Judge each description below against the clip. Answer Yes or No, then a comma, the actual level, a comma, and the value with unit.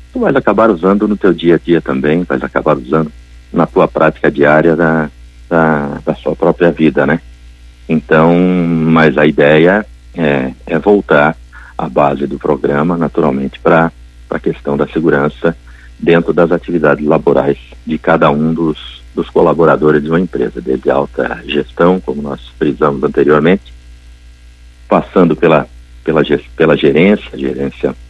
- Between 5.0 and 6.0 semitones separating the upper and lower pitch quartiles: Yes, wide, 5.6 semitones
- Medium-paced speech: Yes, average, 145 wpm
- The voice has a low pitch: Yes, very low, 75 Hz